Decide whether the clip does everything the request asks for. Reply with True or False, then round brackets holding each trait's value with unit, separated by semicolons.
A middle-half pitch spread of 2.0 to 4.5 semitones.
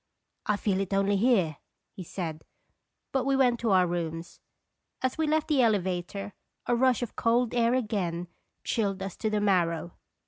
False (5.2 semitones)